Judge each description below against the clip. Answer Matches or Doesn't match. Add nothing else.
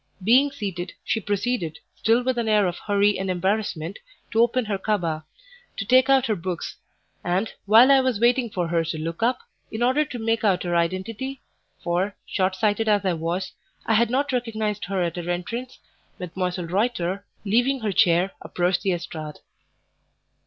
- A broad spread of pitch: Doesn't match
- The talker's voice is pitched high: Matches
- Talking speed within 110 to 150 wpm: Doesn't match